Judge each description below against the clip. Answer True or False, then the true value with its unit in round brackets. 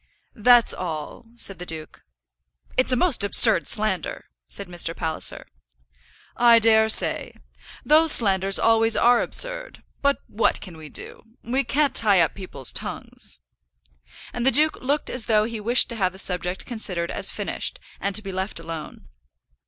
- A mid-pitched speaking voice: False (215 Hz)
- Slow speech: False (160 wpm)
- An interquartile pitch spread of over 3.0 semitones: True (5.0 semitones)